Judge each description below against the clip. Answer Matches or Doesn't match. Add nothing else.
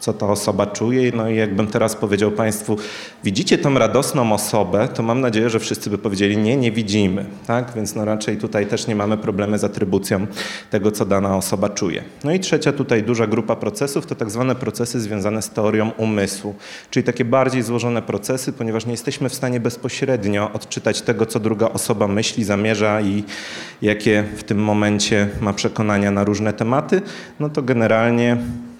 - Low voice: Matches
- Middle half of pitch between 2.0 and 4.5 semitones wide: Matches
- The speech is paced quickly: Matches